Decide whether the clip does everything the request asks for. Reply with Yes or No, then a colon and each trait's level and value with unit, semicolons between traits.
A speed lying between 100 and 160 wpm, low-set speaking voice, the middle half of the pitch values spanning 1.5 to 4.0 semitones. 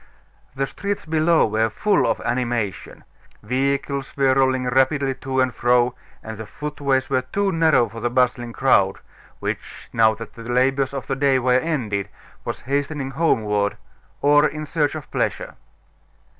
Yes: average, 155 wpm; low, 130 Hz; average, 3.0 semitones